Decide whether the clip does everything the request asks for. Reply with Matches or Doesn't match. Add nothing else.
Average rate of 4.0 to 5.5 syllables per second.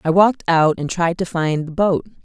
Matches